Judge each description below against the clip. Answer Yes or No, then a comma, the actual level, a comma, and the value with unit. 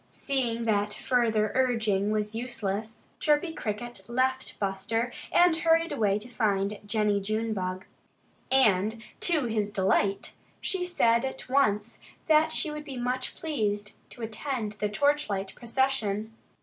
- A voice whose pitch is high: Yes, high, 225 Hz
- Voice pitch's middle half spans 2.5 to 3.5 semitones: No, average, 4.1 semitones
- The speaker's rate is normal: No, slow, 130 wpm